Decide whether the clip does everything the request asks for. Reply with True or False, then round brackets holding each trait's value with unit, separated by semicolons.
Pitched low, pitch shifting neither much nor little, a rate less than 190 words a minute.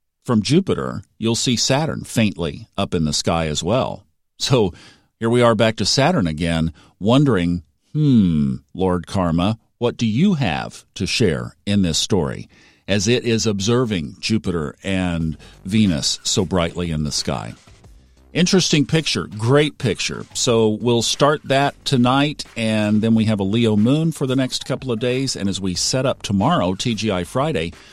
False (110 Hz; 6.0 semitones; 160 wpm)